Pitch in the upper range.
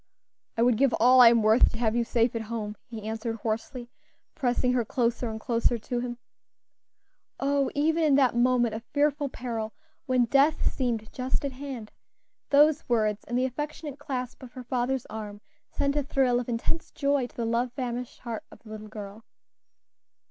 Yes: high, 245 Hz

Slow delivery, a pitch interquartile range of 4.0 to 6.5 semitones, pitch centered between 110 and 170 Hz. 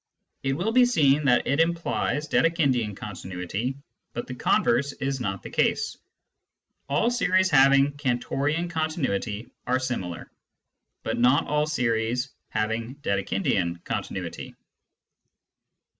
Yes: slow, 115 wpm; average, 5.2 semitones; low, 135 Hz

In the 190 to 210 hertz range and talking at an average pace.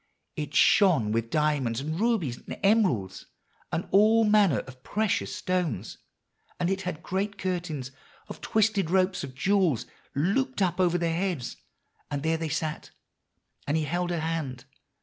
No: medium, 170 Hz; average, 150 wpm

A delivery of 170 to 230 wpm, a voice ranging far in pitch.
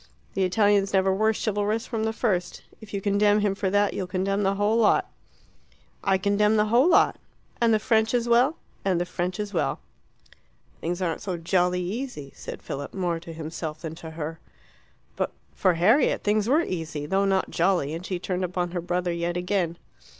No: average, 190 wpm; average, 3.2 semitones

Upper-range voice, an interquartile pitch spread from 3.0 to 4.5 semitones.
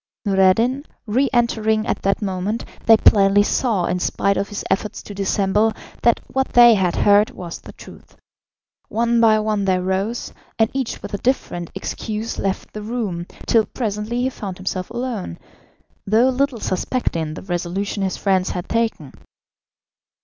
Yes: high, 210 Hz; average, 3.5 semitones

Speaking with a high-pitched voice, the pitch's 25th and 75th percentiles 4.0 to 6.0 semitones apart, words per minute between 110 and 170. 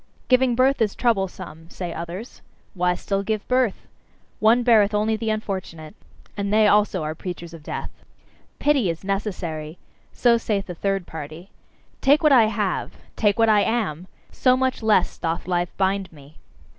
Yes: high, 200 Hz; average, 4.3 semitones; average, 160 wpm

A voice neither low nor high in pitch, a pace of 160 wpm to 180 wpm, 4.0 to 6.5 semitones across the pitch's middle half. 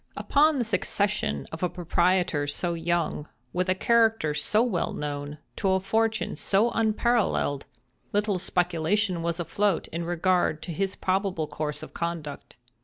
No: medium, 180 Hz; average, 145 wpm; average, 4.3 semitones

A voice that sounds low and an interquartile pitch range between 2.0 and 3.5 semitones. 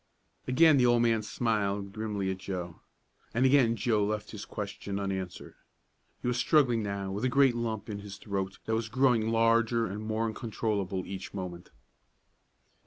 Yes: low, 110 Hz; average, 2.8 semitones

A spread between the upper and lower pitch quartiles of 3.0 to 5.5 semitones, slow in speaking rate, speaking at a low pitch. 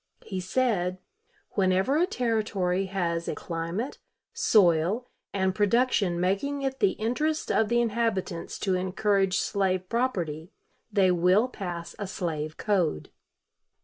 No: average, 4.4 semitones; slow, 120 wpm; high, 195 Hz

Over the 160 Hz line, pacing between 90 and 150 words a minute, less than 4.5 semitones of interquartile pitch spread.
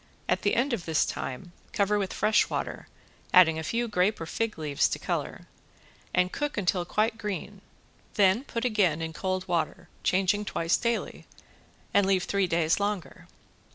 No: high, 190 Hz; average, 165 wpm; average, 3.5 semitones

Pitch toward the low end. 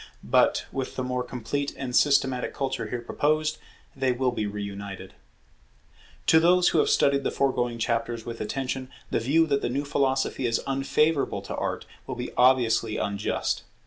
Yes: low, 130 Hz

